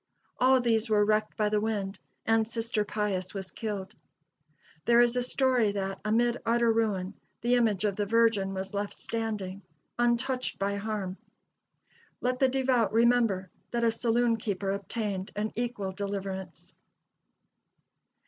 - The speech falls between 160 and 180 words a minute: No, average, 140 wpm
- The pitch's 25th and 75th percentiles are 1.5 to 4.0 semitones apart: Yes, average, 3.0 semitones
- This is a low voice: No, high, 215 Hz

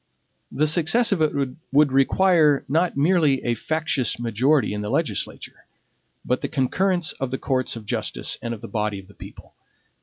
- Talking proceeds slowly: No, average, 175 wpm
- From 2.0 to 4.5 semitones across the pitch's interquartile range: No, average, 5.1 semitones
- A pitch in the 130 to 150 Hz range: Yes, medium, 140 Hz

